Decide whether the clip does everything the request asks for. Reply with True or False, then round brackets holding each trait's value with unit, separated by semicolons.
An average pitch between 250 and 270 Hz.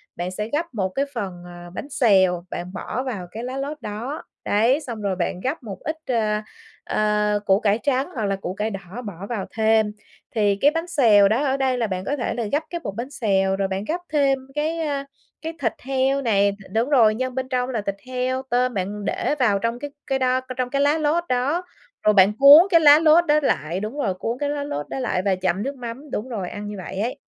False (235 Hz)